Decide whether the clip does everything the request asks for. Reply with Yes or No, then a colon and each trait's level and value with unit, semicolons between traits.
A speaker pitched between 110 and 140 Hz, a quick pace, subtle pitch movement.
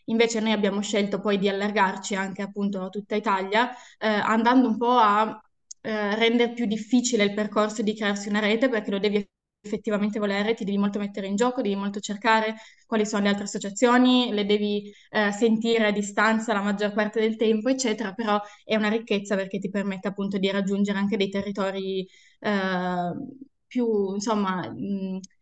No: high, 210 Hz; fast, 175 wpm; narrow, 1.7 semitones